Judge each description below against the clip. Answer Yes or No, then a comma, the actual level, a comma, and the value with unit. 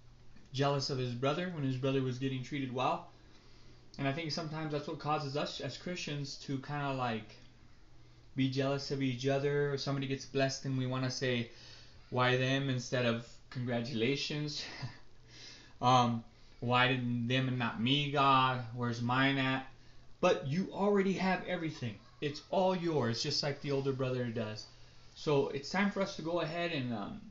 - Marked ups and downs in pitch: No, average, 2.9 semitones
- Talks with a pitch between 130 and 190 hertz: Yes, low, 135 Hz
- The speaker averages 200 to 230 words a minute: No, average, 175 wpm